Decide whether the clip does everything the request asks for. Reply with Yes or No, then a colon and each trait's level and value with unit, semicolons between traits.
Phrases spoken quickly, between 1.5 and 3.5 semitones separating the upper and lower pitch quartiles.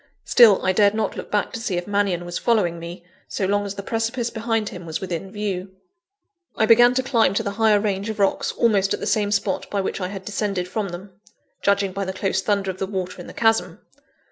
Yes: fast, 235 wpm; narrow, 2.5 semitones